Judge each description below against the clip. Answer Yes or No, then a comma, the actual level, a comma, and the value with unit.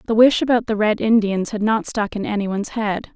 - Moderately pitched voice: No, high, 215 Hz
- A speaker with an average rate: No, fast, 230 wpm